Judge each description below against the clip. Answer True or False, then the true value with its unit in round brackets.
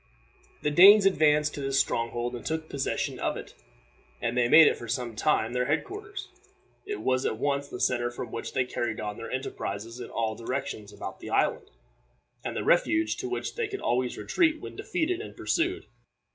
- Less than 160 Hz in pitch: True (140 Hz)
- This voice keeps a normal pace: True (195 wpm)